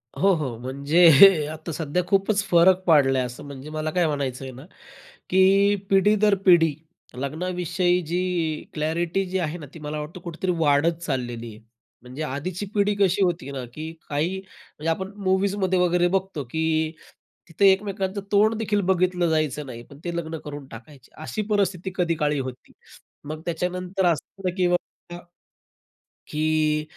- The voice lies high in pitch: No, medium, 170 Hz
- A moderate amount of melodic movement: Yes, average, 3.9 semitones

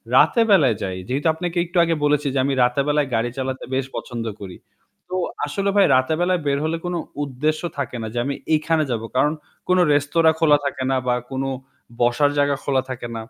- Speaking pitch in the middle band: Yes, medium, 145 Hz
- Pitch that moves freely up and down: No, average, 3.7 semitones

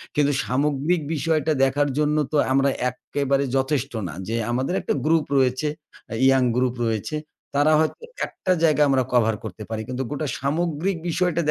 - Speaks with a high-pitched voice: No, medium, 140 Hz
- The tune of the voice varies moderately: Yes, average, 3.1 semitones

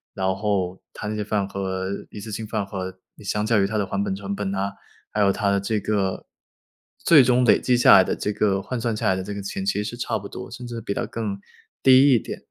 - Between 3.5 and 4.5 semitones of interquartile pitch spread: No, narrow, 2.5 semitones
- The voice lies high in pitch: No, low, 105 Hz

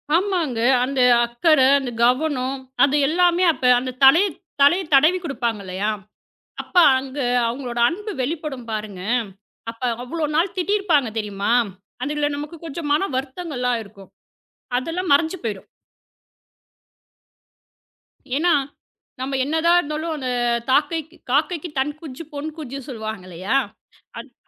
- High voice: Yes, very high, 280 Hz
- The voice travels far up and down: No, average, 4.8 semitones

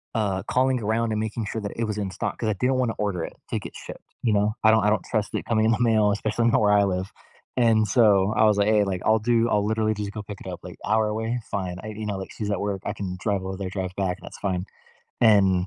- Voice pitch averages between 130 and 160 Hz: No, low, 105 Hz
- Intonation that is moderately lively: No, narrow, 1.9 semitones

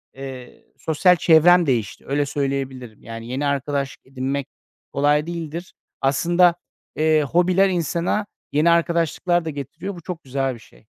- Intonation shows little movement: No, average, 4.1 semitones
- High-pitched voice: No, medium, 150 Hz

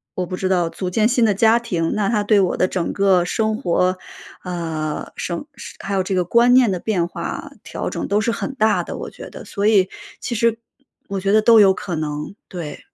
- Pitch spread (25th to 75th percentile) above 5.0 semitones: No, average, 3.5 semitones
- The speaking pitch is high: Yes, high, 195 Hz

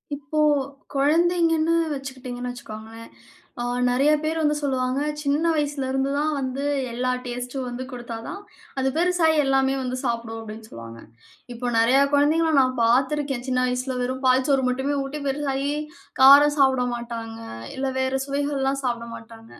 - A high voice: Yes, very high, 265 Hz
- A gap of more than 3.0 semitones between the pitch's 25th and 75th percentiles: No, narrow, 2.6 semitones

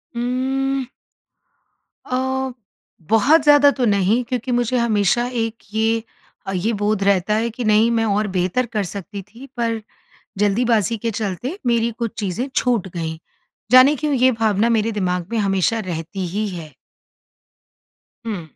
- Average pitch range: Yes, average, 3.5 semitones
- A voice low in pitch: No, high, 225 Hz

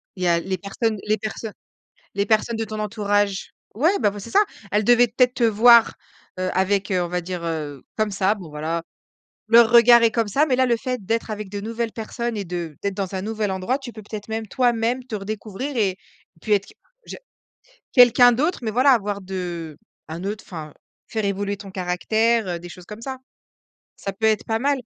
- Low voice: No, high, 210 Hz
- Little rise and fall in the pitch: No, average, 3.6 semitones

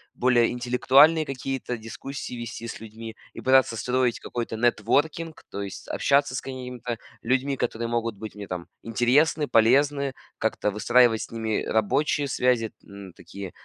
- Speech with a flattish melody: No, average, 3.1 semitones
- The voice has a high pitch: No, low, 120 Hz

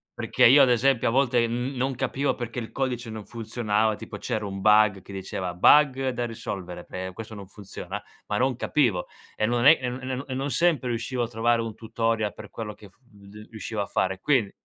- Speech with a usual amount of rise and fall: Yes, average, 3.5 semitones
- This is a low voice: Yes, low, 115 Hz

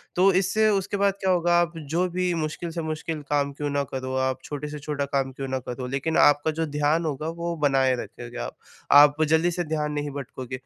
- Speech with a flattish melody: No, average, 3.5 semitones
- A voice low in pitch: No, medium, 150 Hz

